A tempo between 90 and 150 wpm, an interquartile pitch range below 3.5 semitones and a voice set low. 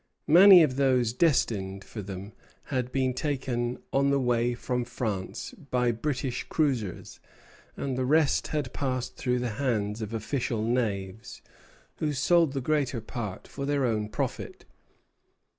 No: average, 140 wpm; average, 3.8 semitones; low, 125 Hz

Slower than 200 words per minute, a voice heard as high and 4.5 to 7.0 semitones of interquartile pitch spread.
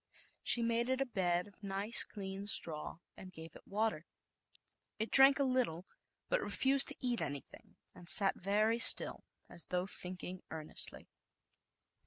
Yes: average, 155 wpm; high, 200 Hz; average, 4.8 semitones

